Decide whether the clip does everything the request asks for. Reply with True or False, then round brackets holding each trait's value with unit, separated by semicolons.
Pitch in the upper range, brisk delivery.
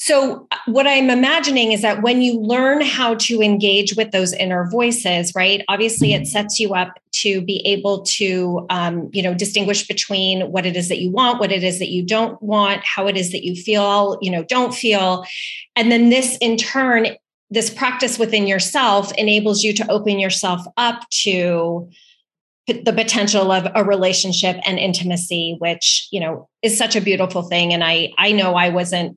False (200 Hz; 185 wpm)